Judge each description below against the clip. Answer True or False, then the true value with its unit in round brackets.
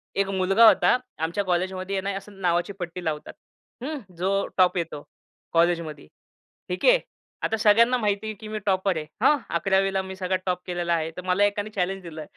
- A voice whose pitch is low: False (190 Hz)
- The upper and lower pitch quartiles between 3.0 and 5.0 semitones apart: False (2.6 semitones)